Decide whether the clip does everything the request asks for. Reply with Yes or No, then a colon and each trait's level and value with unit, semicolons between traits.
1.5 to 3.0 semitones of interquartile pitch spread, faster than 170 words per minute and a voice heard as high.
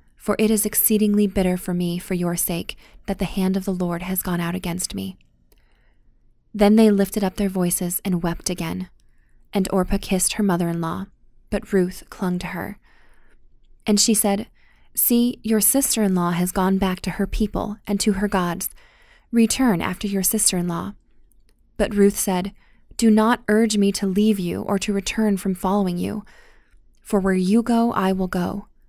Yes: average, 2.7 semitones; average, 185 wpm; high, 195 Hz